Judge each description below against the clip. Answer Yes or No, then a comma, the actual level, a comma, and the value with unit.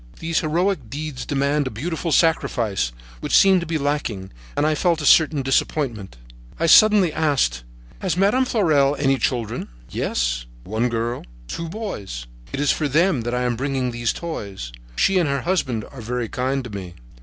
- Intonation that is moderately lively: No, wide, 5.8 semitones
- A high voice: No, medium, 140 Hz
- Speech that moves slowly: No, average, 180 wpm